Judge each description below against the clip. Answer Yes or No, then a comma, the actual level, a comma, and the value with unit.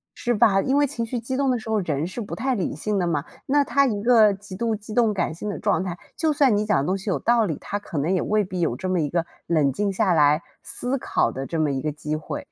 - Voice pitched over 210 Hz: No, high, 205 Hz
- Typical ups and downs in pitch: No, wide, 5.7 semitones